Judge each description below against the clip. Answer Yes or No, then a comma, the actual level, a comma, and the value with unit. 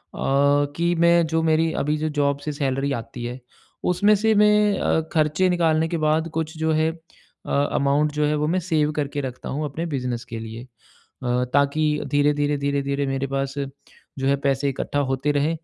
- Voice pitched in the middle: Yes, medium, 150 Hz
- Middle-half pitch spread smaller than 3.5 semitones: Yes, average, 2.7 semitones